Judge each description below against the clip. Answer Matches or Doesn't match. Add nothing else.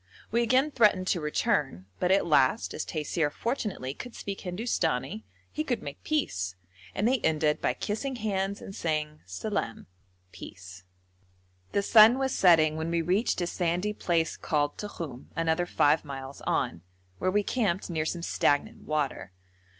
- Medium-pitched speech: Matches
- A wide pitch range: Matches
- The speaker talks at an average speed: Matches